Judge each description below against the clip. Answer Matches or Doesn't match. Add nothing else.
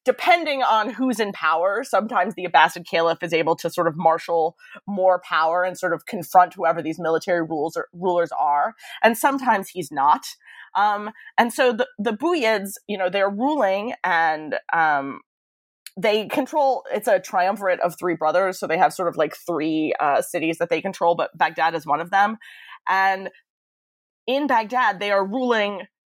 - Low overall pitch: Doesn't match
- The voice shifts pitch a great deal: Doesn't match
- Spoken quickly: Doesn't match